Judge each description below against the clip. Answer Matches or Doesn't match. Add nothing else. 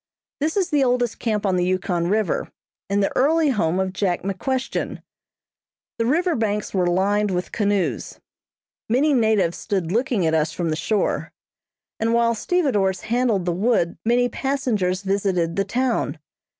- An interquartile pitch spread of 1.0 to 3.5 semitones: Doesn't match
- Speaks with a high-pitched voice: Matches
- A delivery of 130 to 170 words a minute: Matches